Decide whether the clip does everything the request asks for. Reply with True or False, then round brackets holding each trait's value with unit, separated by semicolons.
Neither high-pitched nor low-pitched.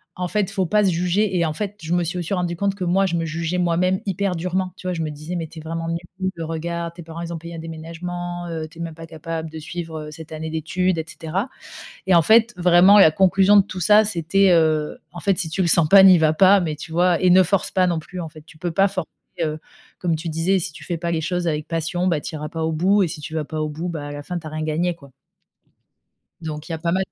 True (170 Hz)